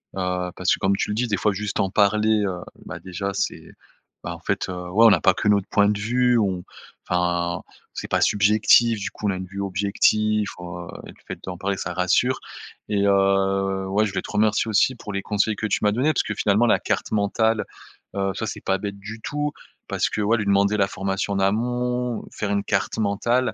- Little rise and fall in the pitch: Yes, narrow, 2.0 semitones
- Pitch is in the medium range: No, low, 100 Hz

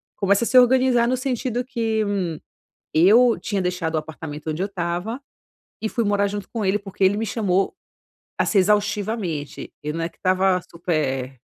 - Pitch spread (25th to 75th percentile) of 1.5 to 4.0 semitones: No, average, 4.6 semitones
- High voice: Yes, high, 200 Hz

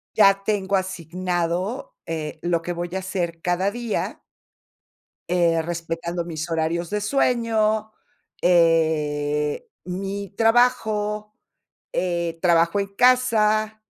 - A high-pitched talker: No, medium, 180 Hz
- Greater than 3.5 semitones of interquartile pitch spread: Yes, average, 4.0 semitones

